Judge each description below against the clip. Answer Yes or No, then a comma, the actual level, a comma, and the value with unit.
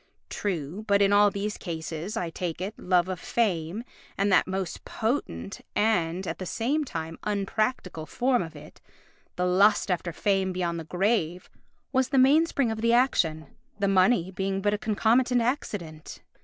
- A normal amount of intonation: Yes, average, 4.2 semitones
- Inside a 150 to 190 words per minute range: Yes, average, 165 wpm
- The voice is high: Yes, high, 195 Hz